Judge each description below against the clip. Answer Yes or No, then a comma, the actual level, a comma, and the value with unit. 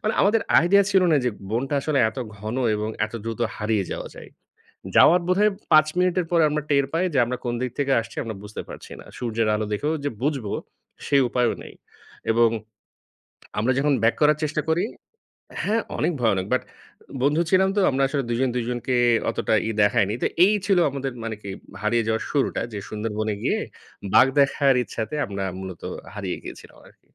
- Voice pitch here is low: Yes, low, 130 Hz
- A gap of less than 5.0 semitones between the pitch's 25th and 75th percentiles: No, wide, 5.6 semitones